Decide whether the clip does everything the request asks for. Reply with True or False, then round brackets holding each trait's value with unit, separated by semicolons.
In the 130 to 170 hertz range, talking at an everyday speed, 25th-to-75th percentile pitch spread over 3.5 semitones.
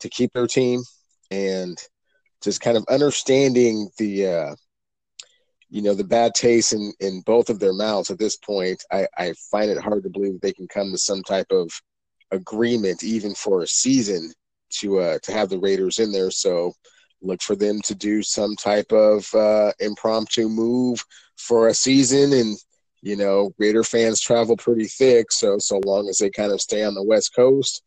False (115 Hz; 185 wpm; 3.9 semitones)